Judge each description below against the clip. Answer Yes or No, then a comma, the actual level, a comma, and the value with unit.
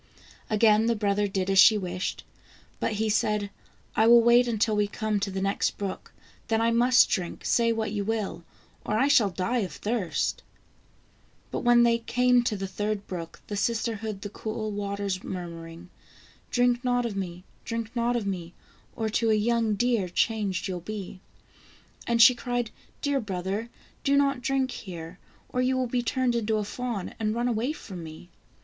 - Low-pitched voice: No, high, 215 Hz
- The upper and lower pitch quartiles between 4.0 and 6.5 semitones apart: No, average, 3.3 semitones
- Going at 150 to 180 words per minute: No, average, 190 wpm